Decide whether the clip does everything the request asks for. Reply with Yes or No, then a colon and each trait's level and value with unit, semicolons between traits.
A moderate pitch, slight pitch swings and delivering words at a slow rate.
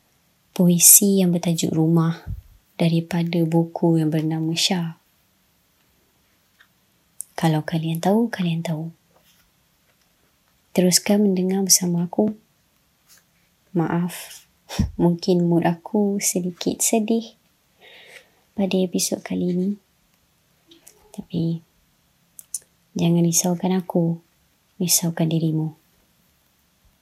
Yes: medium, 170 Hz; narrow, 2.2 semitones; slow, 75 wpm